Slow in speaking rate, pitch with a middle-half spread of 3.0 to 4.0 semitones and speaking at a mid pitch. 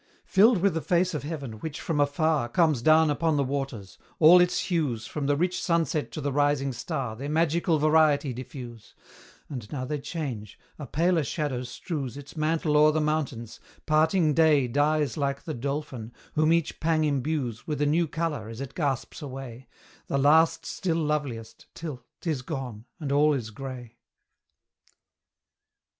No: average, 165 wpm; average, 3.3 semitones; medium, 145 Hz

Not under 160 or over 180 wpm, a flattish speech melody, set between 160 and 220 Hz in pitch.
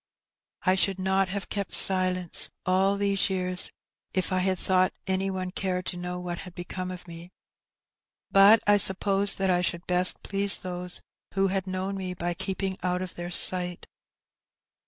Yes: average, 170 wpm; narrow, 1.3 semitones; medium, 185 Hz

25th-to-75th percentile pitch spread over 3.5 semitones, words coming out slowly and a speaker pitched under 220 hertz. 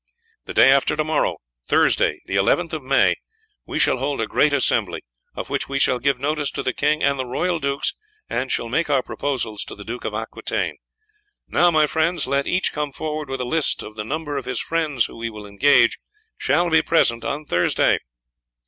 No: average, 3.9 semitones; fast, 205 wpm; medium, 140 Hz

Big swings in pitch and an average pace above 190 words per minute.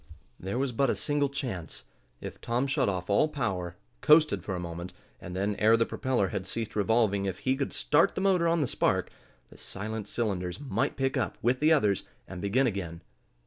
Yes: wide, 6.1 semitones; average, 200 wpm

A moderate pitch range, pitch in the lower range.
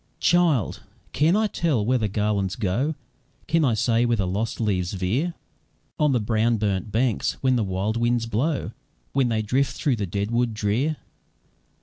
Yes: average, 4.3 semitones; low, 115 Hz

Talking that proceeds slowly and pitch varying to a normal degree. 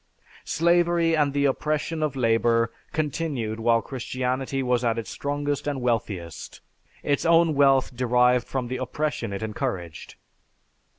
Yes: slow, 130 wpm; average, 4.0 semitones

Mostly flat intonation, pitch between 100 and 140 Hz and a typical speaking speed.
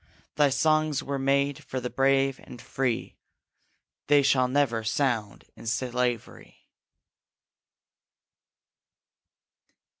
No: narrow, 2.2 semitones; low, 135 Hz; slow, 90 wpm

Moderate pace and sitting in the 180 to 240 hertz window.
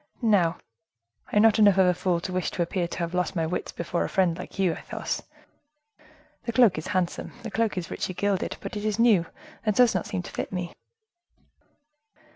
No: fast, 210 wpm; medium, 185 Hz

